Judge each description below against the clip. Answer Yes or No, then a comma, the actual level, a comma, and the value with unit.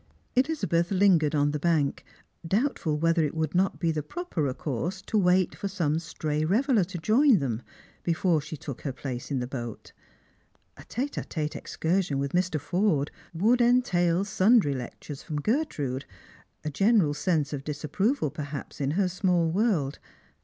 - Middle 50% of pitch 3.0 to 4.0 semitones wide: No, average, 5.1 semitones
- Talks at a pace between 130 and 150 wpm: No, average, 160 wpm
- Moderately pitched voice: Yes, medium, 165 Hz